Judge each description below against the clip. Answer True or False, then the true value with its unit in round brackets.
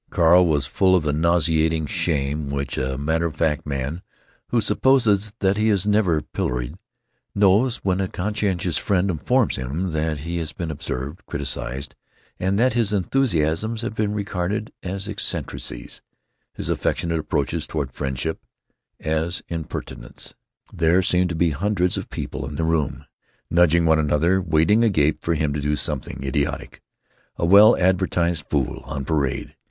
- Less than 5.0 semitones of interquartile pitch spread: True (4.6 semitones)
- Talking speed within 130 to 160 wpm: True (150 wpm)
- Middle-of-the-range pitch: False (85 Hz)